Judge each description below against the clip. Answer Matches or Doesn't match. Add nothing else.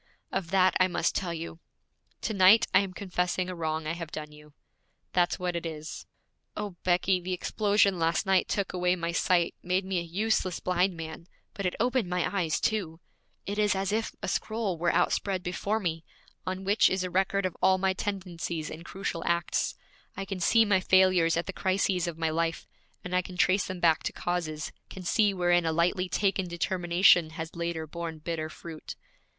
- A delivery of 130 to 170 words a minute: Doesn't match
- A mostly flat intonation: Matches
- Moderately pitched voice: Matches